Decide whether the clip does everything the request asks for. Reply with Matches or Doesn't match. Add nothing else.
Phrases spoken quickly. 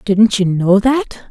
Doesn't match